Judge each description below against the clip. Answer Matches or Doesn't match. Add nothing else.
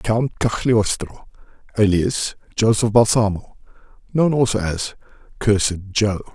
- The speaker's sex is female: Doesn't match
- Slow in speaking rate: Matches